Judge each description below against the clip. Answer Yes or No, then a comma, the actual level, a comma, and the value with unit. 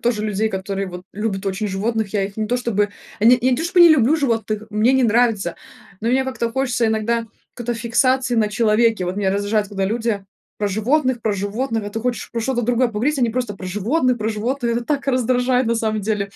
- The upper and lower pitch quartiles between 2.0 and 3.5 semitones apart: Yes, average, 3.1 semitones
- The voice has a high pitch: Yes, high, 225 Hz